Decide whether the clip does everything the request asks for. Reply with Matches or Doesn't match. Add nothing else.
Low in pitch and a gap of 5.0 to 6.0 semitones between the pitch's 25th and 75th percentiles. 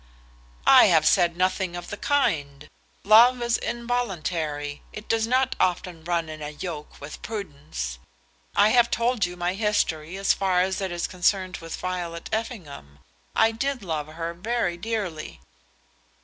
Doesn't match